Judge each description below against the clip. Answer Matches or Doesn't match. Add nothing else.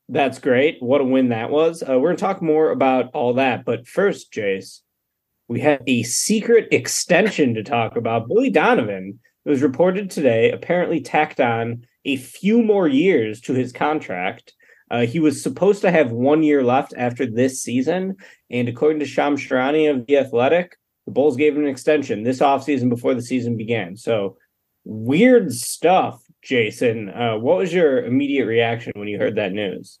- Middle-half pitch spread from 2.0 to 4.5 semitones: Matches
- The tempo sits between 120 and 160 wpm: Doesn't match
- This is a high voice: Doesn't match